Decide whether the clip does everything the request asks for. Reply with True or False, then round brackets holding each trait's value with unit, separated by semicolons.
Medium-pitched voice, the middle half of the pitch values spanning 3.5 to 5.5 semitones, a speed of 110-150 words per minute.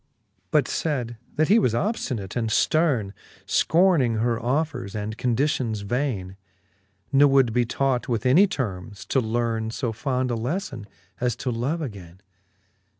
False (120 Hz; 4.2 semitones; 145 wpm)